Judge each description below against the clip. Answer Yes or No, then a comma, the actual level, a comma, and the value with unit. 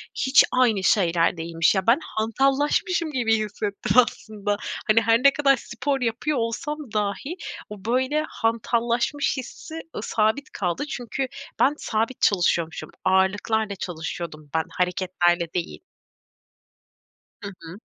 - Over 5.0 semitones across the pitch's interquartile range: Yes, wide, 5.5 semitones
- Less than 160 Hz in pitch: No, high, 225 Hz